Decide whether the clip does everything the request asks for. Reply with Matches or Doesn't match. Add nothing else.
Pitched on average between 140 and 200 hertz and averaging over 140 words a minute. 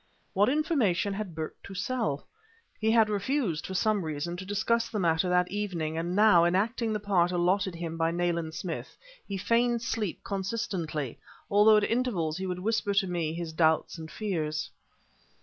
Matches